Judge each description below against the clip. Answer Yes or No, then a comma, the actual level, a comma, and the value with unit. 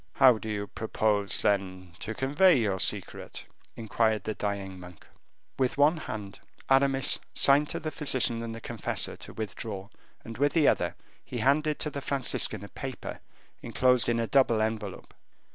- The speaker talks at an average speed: Yes, average, 160 wpm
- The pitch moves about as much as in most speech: Yes, average, 4.8 semitones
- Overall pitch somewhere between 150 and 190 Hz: No, low, 115 Hz